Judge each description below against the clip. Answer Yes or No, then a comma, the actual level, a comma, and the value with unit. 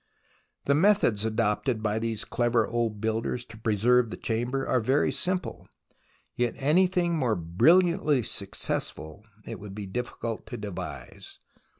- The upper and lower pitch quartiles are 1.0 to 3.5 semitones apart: No, average, 4.1 semitones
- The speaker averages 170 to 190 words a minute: No, slow, 135 wpm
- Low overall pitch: Yes, low, 115 Hz